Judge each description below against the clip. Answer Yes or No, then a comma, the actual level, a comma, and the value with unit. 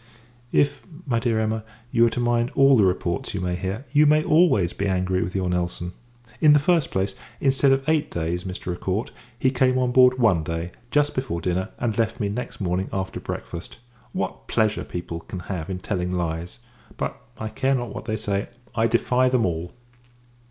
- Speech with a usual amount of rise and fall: No, wide, 6.0 semitones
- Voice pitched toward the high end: No, low, 110 Hz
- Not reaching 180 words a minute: No, average, 195 wpm